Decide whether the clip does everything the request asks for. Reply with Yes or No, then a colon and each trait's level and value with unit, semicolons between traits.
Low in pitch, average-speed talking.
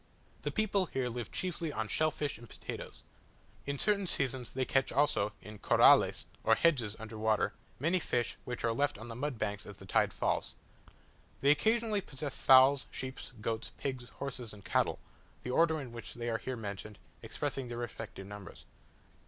Yes: low, 125 Hz; average, 175 wpm